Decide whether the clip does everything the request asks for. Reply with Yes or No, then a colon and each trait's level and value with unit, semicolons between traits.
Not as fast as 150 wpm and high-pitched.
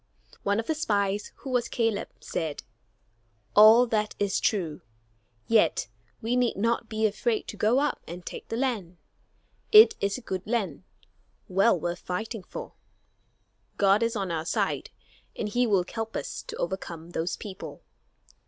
No: average, 155 wpm; high, 210 Hz